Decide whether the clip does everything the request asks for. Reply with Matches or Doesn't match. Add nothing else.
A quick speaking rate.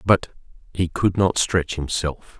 Doesn't match